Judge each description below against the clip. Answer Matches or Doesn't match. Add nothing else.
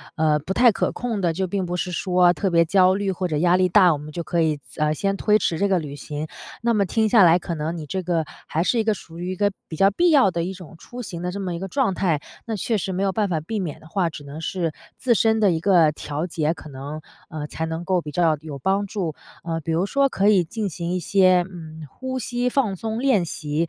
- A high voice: Doesn't match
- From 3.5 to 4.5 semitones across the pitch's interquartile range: Matches